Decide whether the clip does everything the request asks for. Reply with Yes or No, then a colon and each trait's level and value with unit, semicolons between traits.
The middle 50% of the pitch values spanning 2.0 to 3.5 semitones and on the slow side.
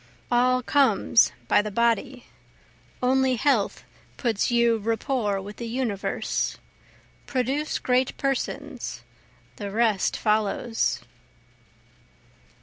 Yes: average, 3.2 semitones; slow, 90 wpm